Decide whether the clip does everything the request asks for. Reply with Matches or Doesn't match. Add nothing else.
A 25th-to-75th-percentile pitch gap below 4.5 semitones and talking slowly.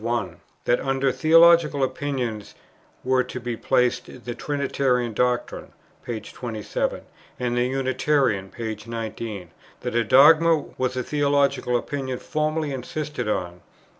Matches